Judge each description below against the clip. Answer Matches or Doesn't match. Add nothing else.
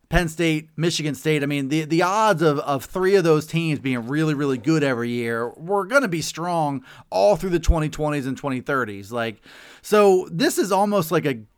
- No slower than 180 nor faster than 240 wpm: Matches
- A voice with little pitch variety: Doesn't match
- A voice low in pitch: Doesn't match